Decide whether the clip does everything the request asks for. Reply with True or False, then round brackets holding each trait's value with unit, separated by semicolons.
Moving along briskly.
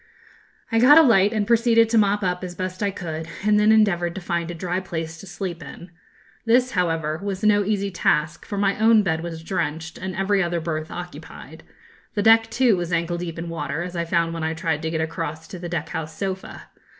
True (220 wpm)